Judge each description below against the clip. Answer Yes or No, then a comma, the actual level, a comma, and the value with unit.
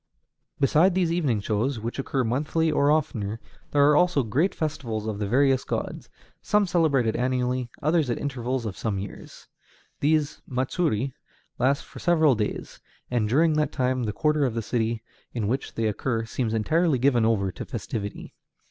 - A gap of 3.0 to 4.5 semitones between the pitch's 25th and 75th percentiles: No, average, 5.0 semitones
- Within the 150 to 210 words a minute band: Yes, average, 165 wpm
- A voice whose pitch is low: Yes, low, 130 Hz